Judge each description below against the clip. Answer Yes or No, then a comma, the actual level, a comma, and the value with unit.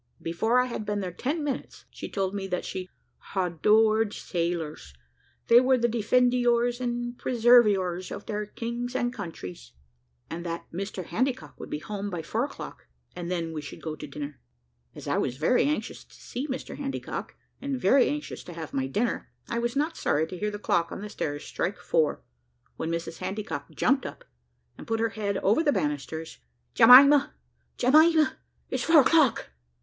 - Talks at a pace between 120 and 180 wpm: Yes, average, 175 wpm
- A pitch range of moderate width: No, wide, 6.3 semitones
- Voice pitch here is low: No, high, 215 Hz